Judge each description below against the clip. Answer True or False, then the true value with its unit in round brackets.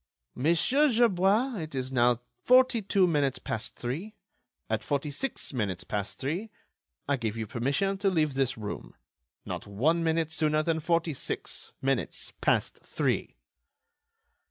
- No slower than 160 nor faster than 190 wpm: False (140 wpm)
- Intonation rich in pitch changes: True (7.1 semitones)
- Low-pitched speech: False (155 Hz)